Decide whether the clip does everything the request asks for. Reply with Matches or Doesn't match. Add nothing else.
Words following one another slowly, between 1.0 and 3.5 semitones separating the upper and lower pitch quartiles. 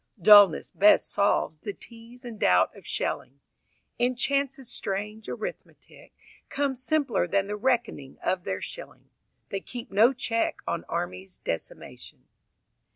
Doesn't match